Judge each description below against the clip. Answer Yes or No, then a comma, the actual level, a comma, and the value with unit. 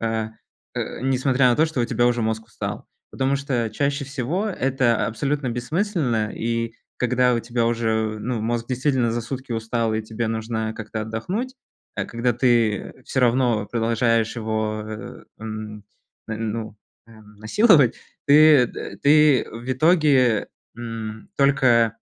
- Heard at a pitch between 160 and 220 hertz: No, low, 120 Hz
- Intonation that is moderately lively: Yes, average, 3.0 semitones